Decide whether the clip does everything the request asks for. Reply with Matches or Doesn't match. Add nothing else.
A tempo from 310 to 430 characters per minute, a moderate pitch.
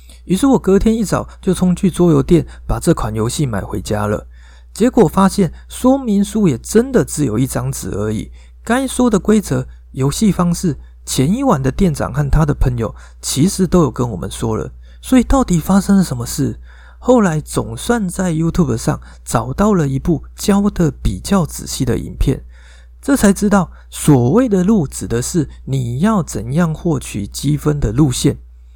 Doesn't match